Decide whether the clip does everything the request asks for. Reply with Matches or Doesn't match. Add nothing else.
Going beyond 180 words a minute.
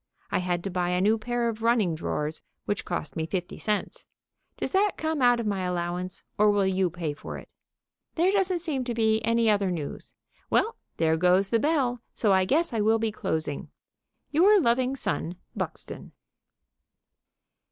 Doesn't match